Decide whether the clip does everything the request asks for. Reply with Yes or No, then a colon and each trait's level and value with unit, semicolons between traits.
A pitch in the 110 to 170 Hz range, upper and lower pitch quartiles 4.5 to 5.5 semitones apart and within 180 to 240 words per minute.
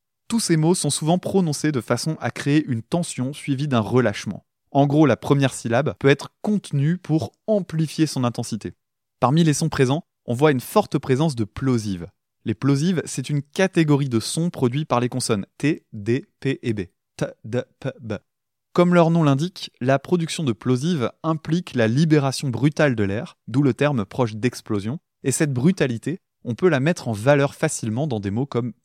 Yes: medium, 140 Hz; average, 4.9 semitones; average, 190 wpm